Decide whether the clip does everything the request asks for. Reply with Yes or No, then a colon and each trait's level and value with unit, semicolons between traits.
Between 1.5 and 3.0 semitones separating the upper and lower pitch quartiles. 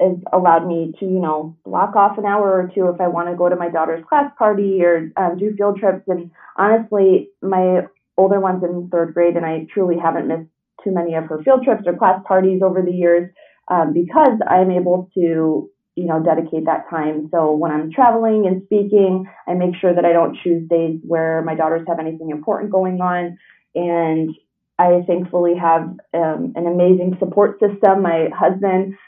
Yes: narrow, 2.5 semitones